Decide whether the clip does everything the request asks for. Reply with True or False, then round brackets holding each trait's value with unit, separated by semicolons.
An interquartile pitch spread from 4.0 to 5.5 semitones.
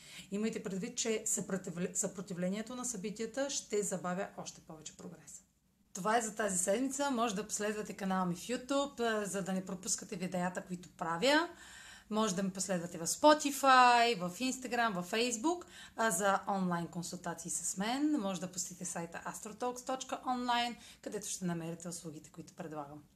True (4.7 semitones)